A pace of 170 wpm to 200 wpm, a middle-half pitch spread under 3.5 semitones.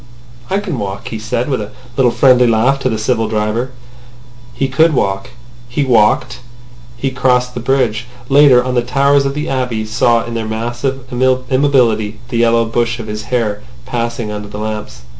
Yes: average, 180 wpm; average, 3.0 semitones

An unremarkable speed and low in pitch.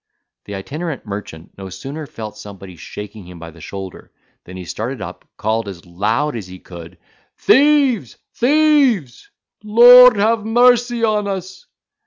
Yes: average, 145 wpm; low, 130 Hz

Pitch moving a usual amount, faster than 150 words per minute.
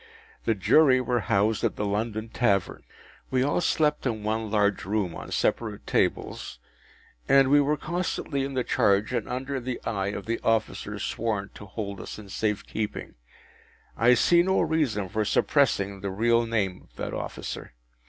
Yes: average, 4.3 semitones; average, 170 wpm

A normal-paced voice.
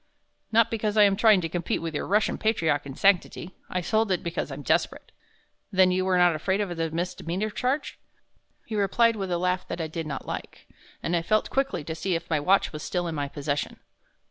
No: fast, 220 wpm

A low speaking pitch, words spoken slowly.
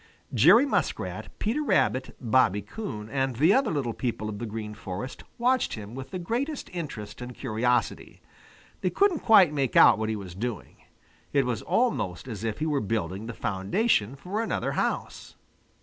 No: low, 125 Hz; average, 170 wpm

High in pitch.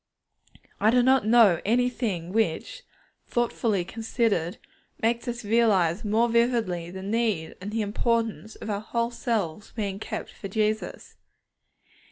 Yes: high, 220 Hz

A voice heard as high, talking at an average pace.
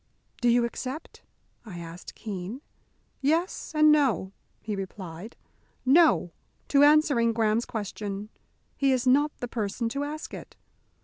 No: high, 235 Hz; slow, 130 wpm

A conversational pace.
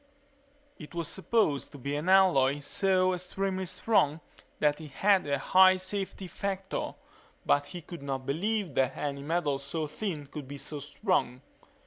Yes: average, 155 wpm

